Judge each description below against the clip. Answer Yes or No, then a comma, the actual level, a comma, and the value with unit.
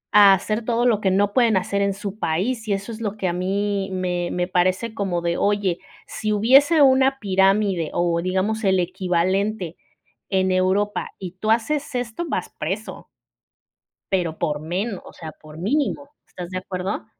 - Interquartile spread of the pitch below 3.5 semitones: Yes, average, 3.1 semitones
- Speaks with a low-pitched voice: No, high, 195 Hz